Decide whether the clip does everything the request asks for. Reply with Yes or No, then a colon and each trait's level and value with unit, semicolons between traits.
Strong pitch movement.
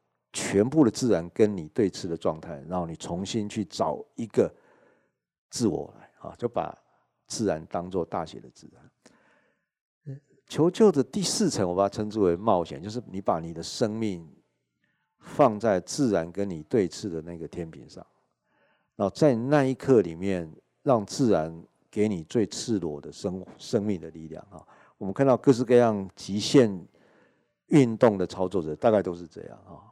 Yes: wide, 6.8 semitones